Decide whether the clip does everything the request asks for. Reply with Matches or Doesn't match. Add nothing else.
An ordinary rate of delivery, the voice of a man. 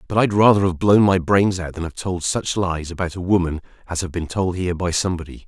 Doesn't match